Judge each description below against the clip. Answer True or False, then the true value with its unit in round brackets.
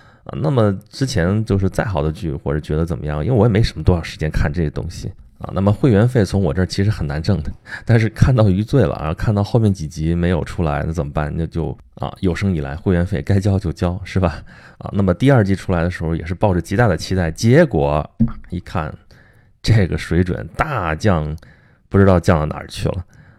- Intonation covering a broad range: False (4.5 semitones)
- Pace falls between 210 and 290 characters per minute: False (325 characters per minute)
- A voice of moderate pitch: False (95 Hz)